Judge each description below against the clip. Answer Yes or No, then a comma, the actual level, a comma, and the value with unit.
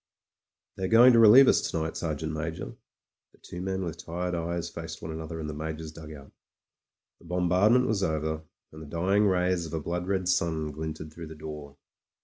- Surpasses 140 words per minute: Yes, average, 195 wpm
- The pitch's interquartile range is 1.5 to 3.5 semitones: Yes, narrow, 2.6 semitones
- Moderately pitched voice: No, very low, 80 Hz